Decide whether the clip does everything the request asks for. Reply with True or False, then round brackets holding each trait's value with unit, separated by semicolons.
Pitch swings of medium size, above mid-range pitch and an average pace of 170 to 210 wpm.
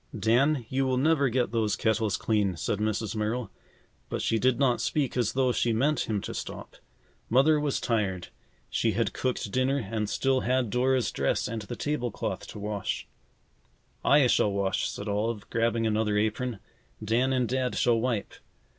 False (3.3 semitones; 115 Hz; 175 wpm)